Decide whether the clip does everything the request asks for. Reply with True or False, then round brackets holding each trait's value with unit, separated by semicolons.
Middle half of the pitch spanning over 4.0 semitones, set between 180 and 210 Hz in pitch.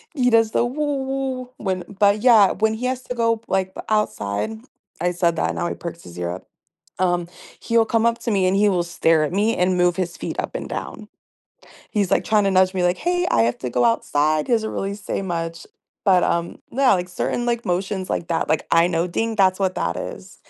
True (4.4 semitones; 190 Hz)